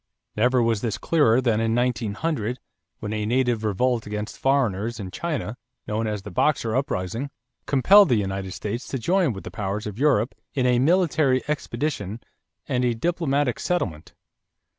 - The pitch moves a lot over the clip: No, average, 4.3 semitones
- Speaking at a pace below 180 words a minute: Yes, average, 160 wpm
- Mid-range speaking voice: No, low, 120 Hz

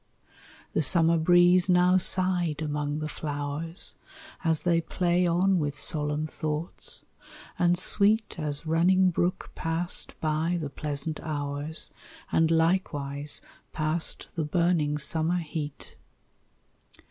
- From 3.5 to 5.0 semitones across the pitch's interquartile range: No, average, 2.8 semitones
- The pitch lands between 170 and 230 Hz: No, medium, 160 Hz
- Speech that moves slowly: Yes, slow, 110 wpm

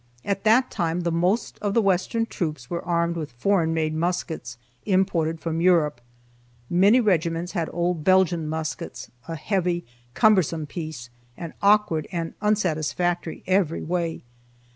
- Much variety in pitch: No, average, 2.9 semitones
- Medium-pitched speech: Yes, medium, 170 Hz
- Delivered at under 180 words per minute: Yes, average, 140 wpm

